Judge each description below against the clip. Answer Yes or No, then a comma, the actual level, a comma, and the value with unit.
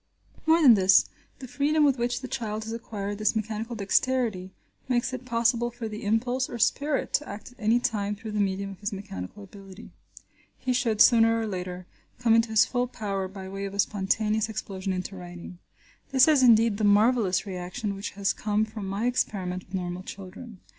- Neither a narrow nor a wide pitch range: Yes, average, 3.4 semitones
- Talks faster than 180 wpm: Yes, average, 195 wpm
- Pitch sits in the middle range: No, high, 215 Hz